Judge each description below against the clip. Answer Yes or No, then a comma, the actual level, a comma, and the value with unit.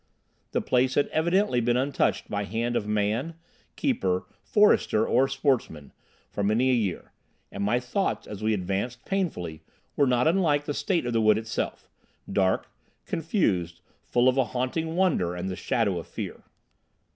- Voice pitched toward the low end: Yes, low, 120 Hz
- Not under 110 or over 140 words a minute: No, average, 155 wpm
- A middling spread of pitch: No, wide, 6.1 semitones